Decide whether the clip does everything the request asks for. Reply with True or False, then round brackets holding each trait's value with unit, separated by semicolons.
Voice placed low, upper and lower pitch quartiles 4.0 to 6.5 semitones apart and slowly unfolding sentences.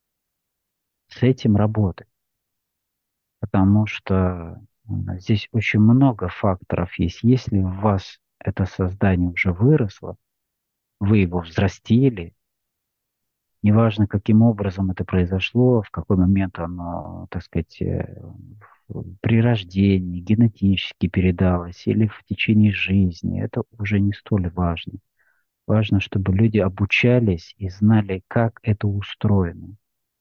False (100 Hz; 3.1 semitones; 105 wpm)